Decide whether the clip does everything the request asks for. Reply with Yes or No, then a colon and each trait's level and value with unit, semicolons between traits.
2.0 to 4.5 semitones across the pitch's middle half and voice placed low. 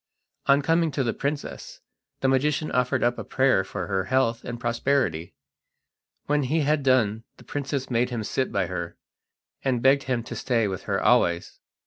Yes: average, 3.8 semitones; low, 125 Hz